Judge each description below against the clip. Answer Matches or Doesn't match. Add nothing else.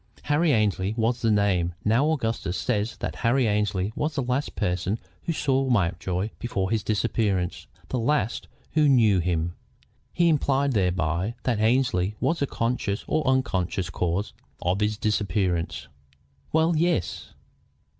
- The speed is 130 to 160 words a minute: Matches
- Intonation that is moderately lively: Doesn't match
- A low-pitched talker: Matches